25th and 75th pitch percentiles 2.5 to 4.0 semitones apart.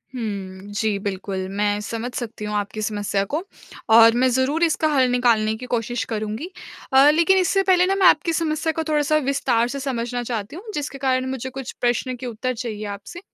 No: wide, 5.6 semitones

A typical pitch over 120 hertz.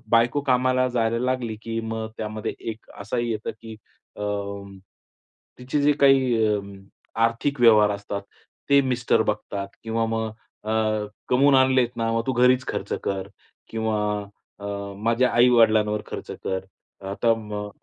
No: low, 115 Hz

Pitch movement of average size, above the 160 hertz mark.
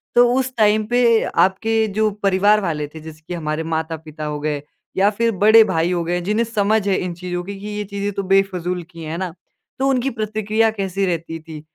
Yes: average, 4.7 semitones; high, 190 Hz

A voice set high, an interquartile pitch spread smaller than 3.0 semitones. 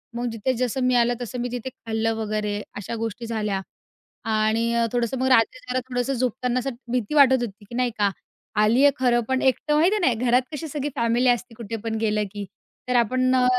Yes: high, 240 Hz; narrow, 2.4 semitones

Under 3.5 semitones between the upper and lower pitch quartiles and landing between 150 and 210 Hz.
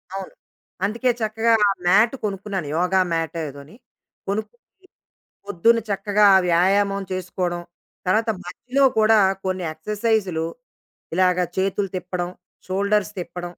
Yes: average, 3.1 semitones; high, 195 Hz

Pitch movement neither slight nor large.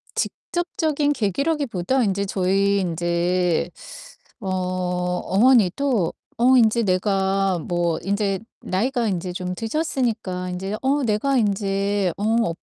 Yes: average, 4.5 semitones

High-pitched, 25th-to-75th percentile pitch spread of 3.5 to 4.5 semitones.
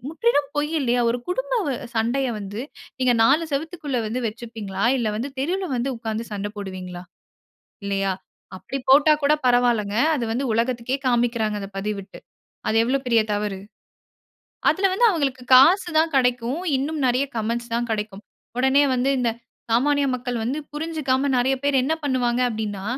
Yes: high, 245 Hz; average, 4.1 semitones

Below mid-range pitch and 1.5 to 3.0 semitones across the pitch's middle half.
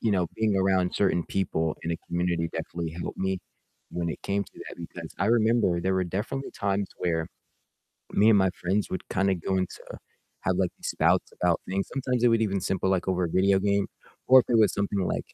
Yes: very low, 95 Hz; narrow, 2.5 semitones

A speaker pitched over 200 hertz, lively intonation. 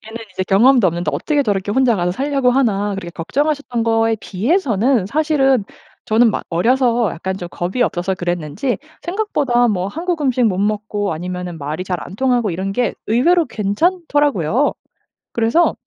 Yes: high, 225 Hz; wide, 6.1 semitones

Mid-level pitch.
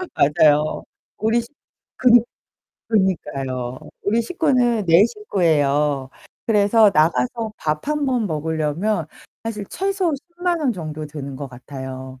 Yes: medium, 175 Hz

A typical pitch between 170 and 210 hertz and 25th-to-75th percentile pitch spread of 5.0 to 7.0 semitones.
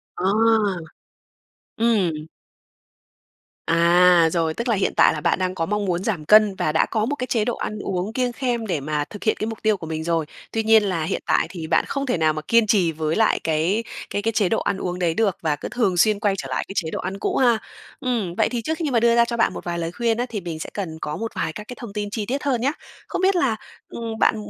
Yes: high, 205 Hz; average, 5.3 semitones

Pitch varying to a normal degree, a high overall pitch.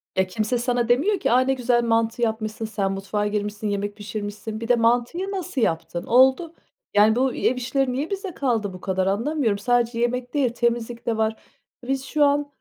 Yes: average, 3.5 semitones; high, 235 Hz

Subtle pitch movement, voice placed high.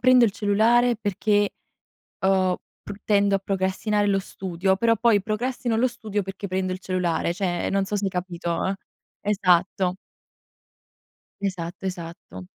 Yes: narrow, 2.3 semitones; high, 195 Hz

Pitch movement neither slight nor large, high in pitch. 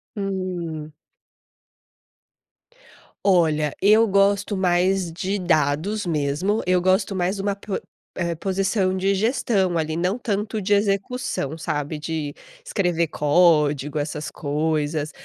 No: average, 4.1 semitones; medium, 180 Hz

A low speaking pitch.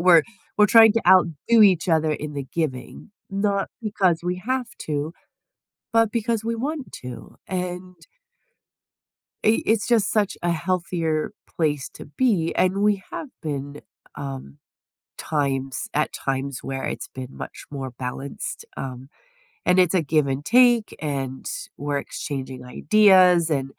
No: medium, 165 Hz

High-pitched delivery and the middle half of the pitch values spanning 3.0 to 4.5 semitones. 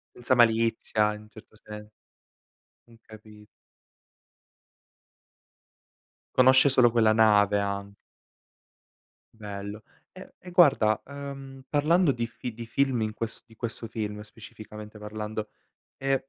No: low, 110 Hz; average, 3.4 semitones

